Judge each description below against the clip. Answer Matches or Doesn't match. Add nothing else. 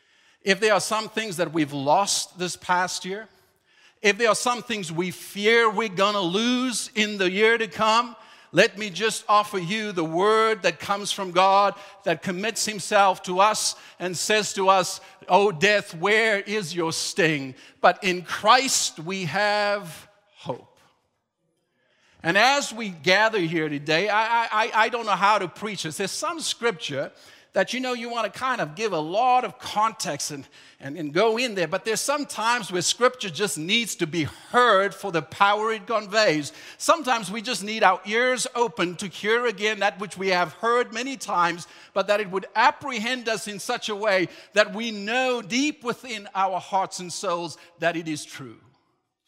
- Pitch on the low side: Doesn't match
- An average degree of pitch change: Matches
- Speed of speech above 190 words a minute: Doesn't match